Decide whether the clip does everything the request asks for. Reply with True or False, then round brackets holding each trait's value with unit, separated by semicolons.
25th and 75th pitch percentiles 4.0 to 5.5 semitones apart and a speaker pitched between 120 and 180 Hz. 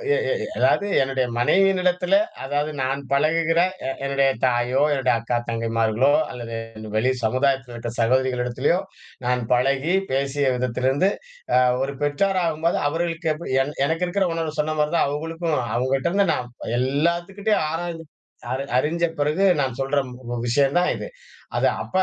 True (4.6 semitones; 140 Hz)